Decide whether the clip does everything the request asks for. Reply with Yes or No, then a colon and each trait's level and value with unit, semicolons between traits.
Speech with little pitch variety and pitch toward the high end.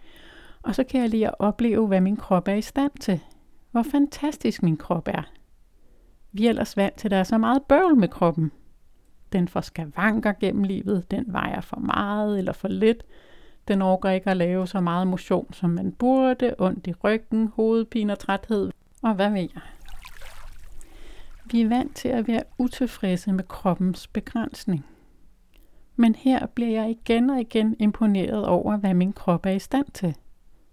No: average, 3.8 semitones; high, 210 Hz